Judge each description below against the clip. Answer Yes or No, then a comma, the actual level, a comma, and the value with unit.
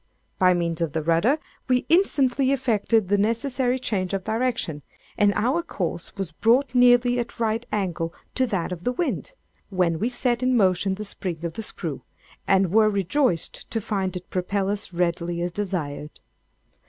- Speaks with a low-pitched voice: No, high, 205 Hz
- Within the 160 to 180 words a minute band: Yes, average, 170 wpm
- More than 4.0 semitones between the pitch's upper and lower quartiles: Yes, wide, 5.6 semitones